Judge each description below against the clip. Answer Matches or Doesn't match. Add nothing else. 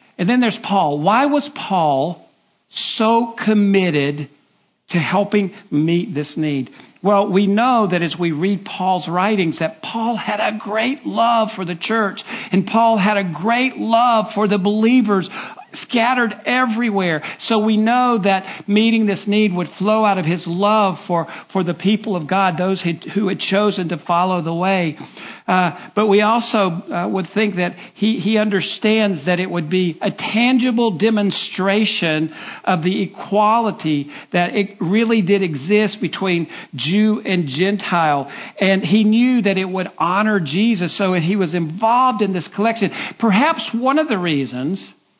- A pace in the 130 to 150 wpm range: Doesn't match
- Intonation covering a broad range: Doesn't match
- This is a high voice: Matches